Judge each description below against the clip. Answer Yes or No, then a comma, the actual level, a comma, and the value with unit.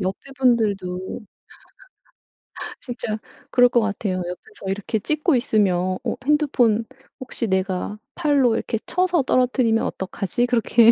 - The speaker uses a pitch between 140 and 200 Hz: No, high, 230 Hz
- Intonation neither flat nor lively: Yes, average, 4.8 semitones